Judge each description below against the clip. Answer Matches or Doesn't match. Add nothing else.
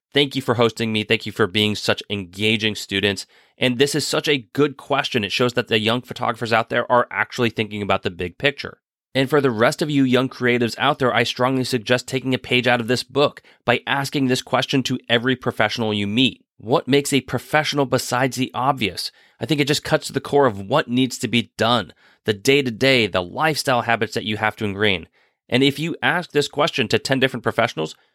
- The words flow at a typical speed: Doesn't match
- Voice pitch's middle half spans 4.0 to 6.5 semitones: Doesn't match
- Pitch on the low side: Matches